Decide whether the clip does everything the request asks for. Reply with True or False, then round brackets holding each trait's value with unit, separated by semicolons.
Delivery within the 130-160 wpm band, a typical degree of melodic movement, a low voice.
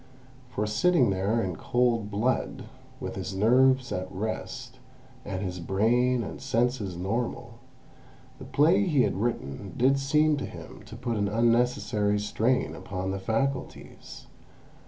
True (135 wpm; 4.2 semitones; 115 Hz)